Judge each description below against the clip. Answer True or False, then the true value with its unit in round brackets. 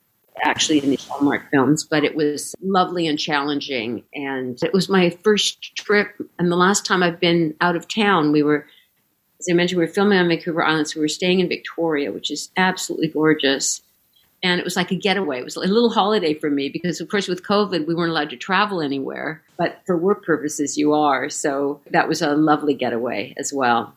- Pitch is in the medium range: True (160 Hz)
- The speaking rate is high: True (215 wpm)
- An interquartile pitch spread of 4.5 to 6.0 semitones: False (3.6 semitones)